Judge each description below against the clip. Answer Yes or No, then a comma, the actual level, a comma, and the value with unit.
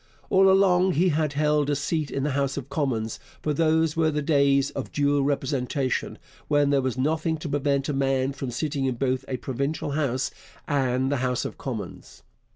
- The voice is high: No, medium, 140 Hz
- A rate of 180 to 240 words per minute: Yes, average, 185 wpm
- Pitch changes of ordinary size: No, narrow, 2.3 semitones